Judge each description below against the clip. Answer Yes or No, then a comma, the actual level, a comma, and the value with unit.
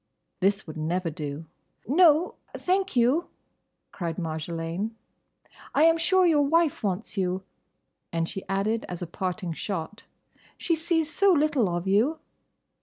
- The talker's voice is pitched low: No, high, 205 Hz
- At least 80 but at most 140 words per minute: Yes, slow, 135 wpm